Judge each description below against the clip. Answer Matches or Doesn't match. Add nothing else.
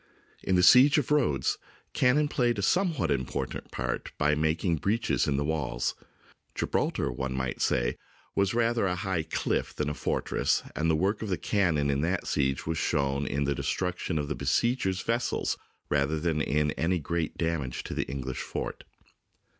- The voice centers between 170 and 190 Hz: Doesn't match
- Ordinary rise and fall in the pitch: Doesn't match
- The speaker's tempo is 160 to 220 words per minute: Matches